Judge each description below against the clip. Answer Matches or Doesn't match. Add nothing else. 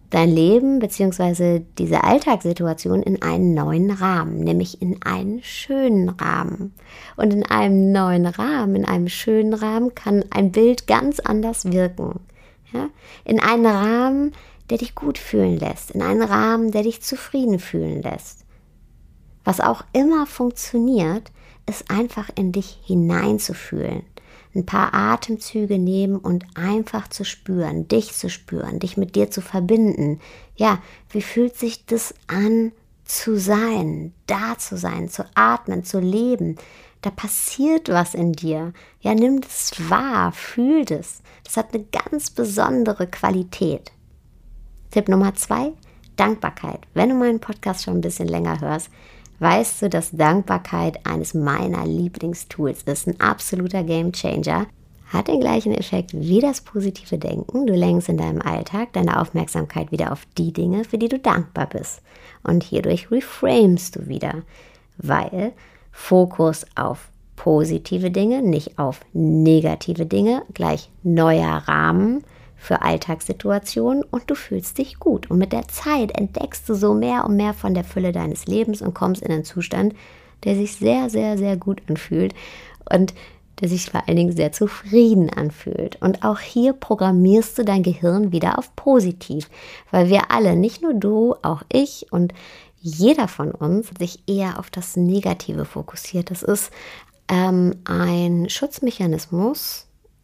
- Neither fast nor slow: Matches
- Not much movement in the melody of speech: Doesn't match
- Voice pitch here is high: Matches